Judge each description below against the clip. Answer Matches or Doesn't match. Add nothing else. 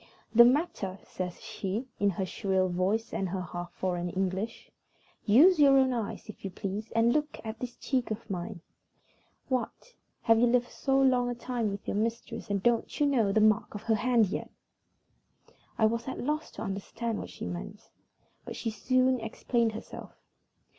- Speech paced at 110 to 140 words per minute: Doesn't match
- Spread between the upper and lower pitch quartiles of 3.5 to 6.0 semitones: Matches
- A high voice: Matches